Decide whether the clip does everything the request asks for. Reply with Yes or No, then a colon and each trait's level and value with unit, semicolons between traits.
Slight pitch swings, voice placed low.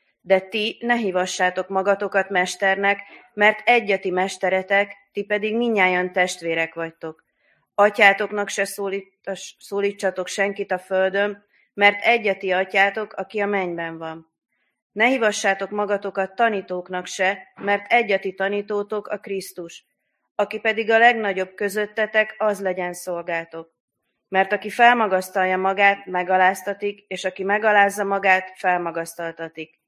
No: narrow, 1.8 semitones; high, 195 Hz